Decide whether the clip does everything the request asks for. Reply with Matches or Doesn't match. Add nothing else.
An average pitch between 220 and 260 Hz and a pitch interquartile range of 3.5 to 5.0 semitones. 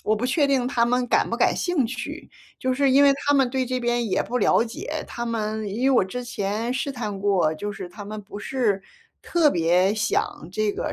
Matches